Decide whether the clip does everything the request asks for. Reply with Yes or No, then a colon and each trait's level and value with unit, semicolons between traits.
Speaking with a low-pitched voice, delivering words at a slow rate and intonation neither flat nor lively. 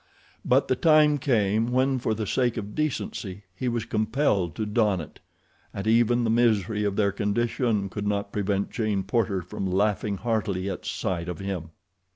No: low, 105 Hz; average, 175 wpm; average, 3.2 semitones